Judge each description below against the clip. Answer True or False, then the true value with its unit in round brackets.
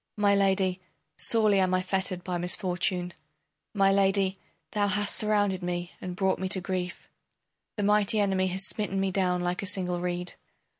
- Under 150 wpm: False (165 wpm)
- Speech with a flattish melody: True (1.8 semitones)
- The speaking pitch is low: False (190 Hz)